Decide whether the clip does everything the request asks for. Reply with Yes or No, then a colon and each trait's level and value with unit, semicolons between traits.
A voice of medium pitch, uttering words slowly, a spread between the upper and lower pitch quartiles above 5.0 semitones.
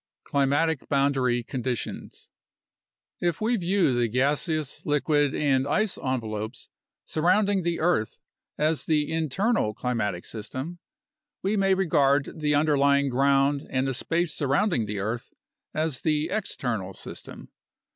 No: medium, 145 Hz; slow, 120 wpm; average, 4.2 semitones